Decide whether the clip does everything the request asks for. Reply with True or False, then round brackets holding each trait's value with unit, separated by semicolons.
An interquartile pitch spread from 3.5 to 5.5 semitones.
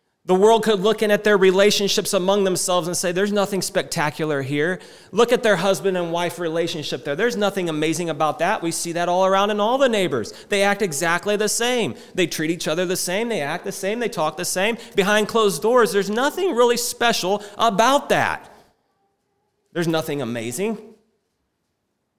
True (3.9 semitones)